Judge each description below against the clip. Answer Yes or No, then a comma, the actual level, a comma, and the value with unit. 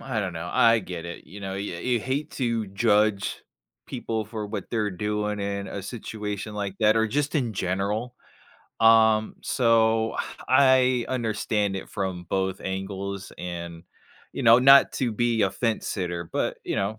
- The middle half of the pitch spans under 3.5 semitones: Yes, average, 2.9 semitones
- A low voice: Yes, low, 105 Hz